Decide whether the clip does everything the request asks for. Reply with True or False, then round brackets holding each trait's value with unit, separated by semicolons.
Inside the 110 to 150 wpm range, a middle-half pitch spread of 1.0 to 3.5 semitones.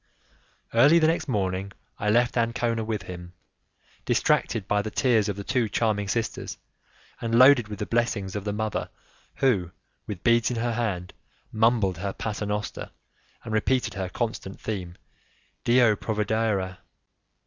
True (140 wpm; 2.9 semitones)